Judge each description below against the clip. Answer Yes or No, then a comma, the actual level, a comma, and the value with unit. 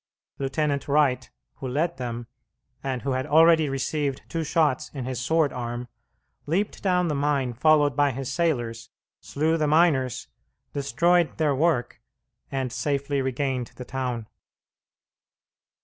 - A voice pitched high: No, medium, 140 Hz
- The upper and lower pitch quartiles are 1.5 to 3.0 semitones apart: No, average, 3.4 semitones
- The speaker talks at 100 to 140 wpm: Yes, slow, 135 wpm